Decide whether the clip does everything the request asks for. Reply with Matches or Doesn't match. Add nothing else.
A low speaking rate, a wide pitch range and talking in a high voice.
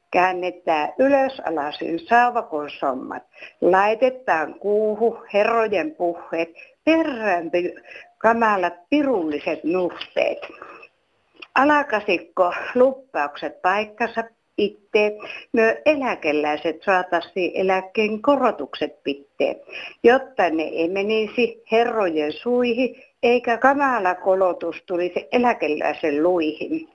Matches